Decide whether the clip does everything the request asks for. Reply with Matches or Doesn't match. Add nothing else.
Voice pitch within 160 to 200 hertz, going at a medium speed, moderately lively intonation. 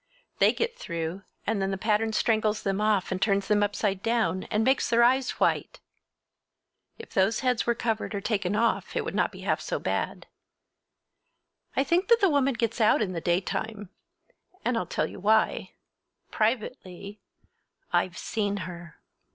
Doesn't match